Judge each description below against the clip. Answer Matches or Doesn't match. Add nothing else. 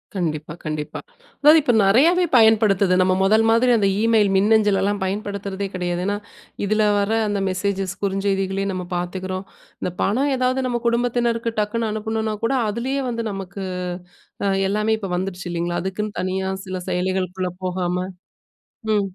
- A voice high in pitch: Matches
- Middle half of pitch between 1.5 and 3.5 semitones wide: Matches